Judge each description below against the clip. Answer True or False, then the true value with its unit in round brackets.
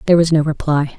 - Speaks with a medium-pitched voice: True (155 Hz)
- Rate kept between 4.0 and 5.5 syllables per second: False (7.2 syllables/s)